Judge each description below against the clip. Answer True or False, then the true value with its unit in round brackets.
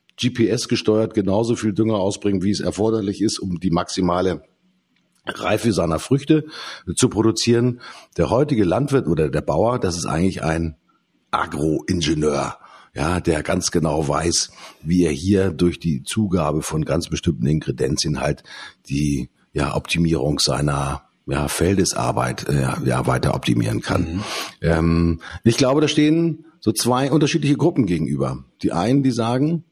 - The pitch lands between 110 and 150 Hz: False (95 Hz)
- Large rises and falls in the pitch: True (7.0 semitones)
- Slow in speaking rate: False (140 wpm)